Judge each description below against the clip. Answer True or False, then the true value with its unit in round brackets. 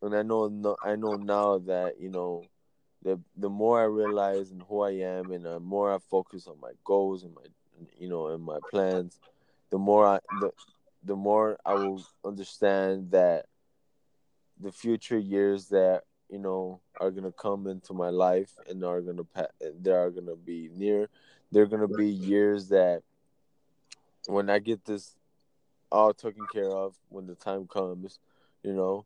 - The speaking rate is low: False (180 wpm)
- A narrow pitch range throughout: True (2.0 semitones)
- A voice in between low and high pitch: False (100 Hz)